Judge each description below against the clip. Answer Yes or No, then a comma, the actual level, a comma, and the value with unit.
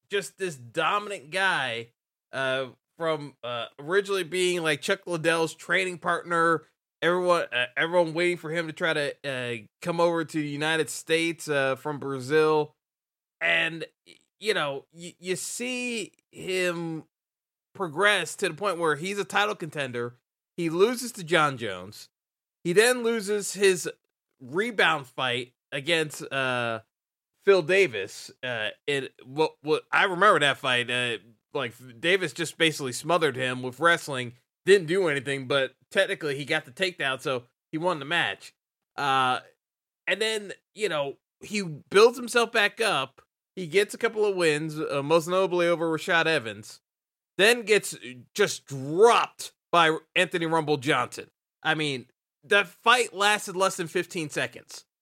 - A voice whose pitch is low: No, medium, 165 Hz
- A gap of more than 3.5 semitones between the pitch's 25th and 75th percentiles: Yes, wide, 5.4 semitones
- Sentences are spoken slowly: No, average, 150 wpm